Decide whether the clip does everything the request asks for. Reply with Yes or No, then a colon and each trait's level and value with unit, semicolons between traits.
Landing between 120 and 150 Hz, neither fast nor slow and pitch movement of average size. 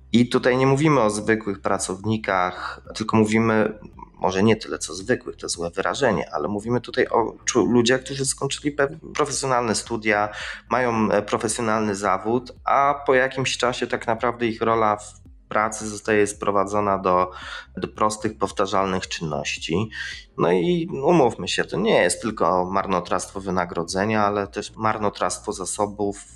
No: low, 110 Hz; average, 140 wpm; average, 3.5 semitones